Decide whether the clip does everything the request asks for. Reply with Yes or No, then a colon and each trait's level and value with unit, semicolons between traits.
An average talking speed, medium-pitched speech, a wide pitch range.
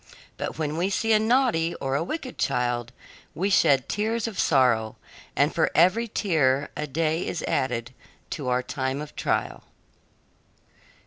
Yes: average, 150 wpm; medium, 155 Hz; wide, 7.2 semitones